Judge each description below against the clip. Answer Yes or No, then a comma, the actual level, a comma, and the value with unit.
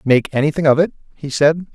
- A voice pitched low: No, medium, 150 Hz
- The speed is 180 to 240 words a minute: Yes, fast, 205 wpm